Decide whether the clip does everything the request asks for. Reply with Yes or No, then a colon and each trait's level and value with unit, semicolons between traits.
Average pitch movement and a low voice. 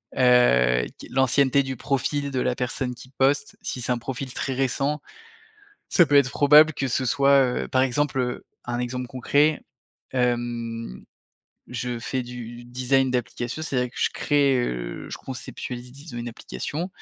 No: narrow, 2.2 semitones; low, 130 Hz